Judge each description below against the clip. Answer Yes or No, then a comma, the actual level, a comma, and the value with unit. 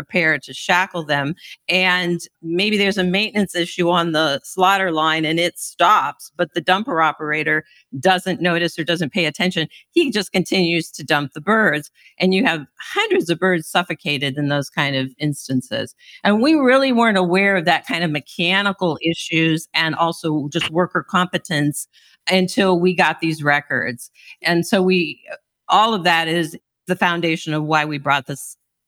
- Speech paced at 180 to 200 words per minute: No, average, 170 wpm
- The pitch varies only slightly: No, average, 3.2 semitones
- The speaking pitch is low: No, medium, 170 Hz